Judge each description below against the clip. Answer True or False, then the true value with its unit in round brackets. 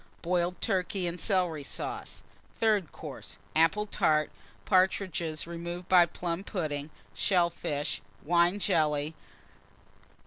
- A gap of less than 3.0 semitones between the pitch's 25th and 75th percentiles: True (2.6 semitones)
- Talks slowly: True (105 wpm)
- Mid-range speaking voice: True (175 Hz)